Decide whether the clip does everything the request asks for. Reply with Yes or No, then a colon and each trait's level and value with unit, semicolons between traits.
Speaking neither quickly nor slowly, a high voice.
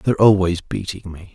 No: average, 180 wpm; very low, 95 Hz